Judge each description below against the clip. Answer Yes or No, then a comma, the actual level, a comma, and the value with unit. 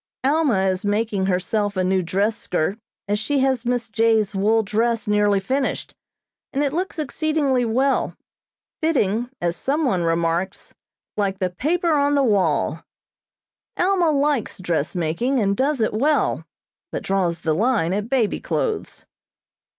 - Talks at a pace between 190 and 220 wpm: No, average, 145 wpm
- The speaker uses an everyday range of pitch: No, wide, 6.2 semitones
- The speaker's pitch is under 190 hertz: No, high, 220 Hz